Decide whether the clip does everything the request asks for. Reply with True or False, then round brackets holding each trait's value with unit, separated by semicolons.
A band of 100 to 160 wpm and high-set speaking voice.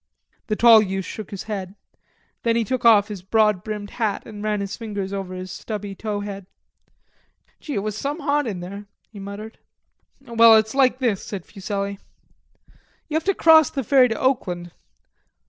False (180 wpm; 210 Hz)